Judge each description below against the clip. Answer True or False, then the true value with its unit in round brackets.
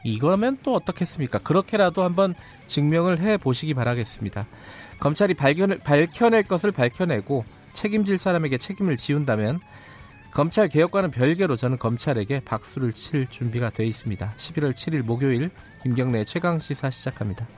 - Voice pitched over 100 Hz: True (140 Hz)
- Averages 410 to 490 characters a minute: False (360 characters per minute)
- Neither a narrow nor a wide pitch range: False (7.3 semitones)